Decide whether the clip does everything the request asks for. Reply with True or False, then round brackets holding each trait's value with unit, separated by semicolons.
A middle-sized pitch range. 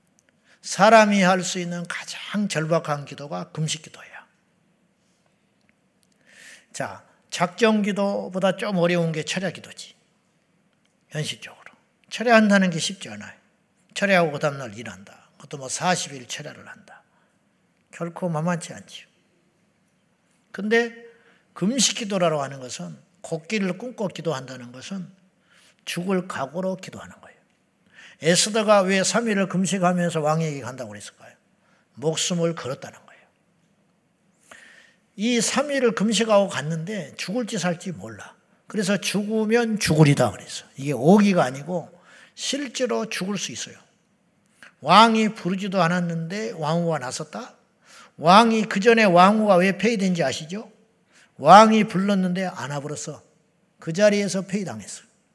True (4.2 semitones)